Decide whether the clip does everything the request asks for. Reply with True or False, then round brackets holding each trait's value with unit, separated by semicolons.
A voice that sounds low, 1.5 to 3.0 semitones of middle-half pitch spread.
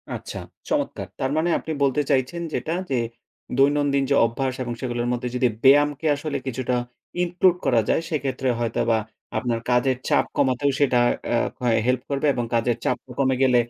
True (130 Hz; 2.7 semitones)